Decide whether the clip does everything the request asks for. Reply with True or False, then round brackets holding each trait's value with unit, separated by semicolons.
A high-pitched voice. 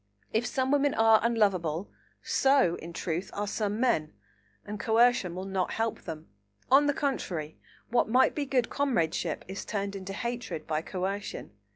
True (210 Hz)